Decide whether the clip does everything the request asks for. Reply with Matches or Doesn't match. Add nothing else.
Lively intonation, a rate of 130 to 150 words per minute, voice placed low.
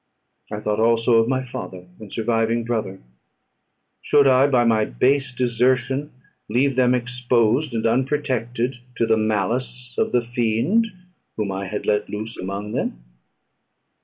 Doesn't match